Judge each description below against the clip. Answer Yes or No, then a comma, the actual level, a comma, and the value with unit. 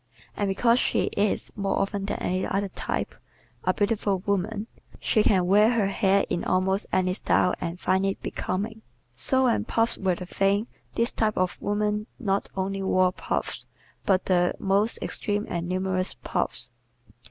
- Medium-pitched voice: No, high, 195 Hz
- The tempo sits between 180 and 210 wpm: No, average, 165 wpm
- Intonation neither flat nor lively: No, narrow, 2.1 semitones